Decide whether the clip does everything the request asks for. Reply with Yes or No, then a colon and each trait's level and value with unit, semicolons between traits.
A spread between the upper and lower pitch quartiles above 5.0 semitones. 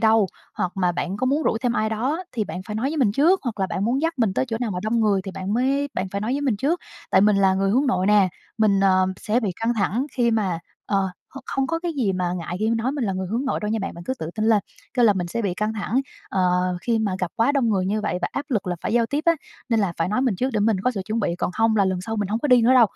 No: average, 4.3 semitones